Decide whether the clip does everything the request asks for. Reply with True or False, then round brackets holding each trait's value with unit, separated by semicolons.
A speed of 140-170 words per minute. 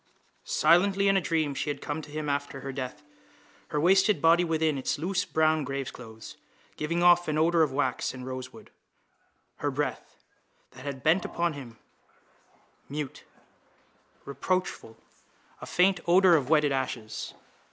True (145 wpm)